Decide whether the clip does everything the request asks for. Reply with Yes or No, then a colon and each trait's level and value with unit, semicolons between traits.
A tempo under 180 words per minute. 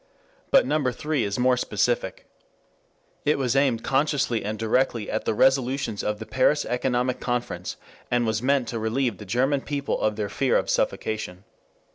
Yes: average, 165 wpm